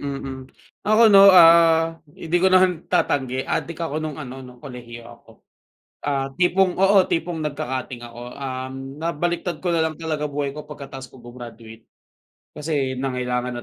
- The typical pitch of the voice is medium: Yes, medium, 145 Hz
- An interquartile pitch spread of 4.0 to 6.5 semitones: Yes, average, 4.6 semitones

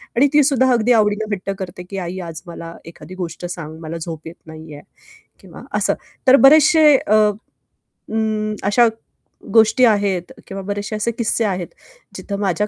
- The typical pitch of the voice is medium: No, high, 200 Hz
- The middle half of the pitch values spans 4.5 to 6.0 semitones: Yes, average, 5.1 semitones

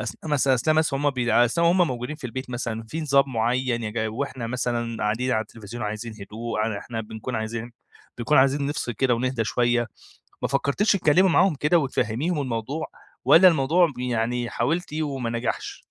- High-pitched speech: No, low, 125 Hz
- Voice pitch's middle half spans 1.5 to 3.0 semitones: No, average, 3.8 semitones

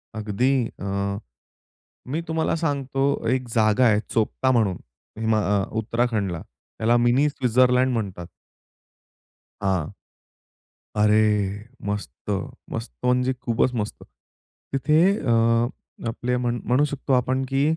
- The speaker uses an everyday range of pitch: Yes, average, 3.8 semitones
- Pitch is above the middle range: No, low, 120 Hz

